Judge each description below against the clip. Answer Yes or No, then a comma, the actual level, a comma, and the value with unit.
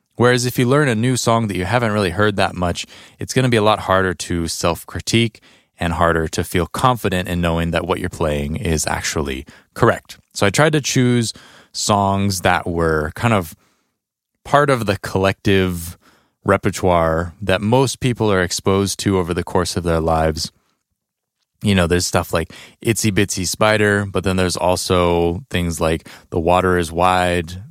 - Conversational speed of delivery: Yes, average, 180 wpm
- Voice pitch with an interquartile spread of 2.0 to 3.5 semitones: No, average, 3.9 semitones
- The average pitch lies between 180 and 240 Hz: No, very low, 95 Hz